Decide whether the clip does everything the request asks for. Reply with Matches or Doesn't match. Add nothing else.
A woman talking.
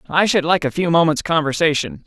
Doesn't match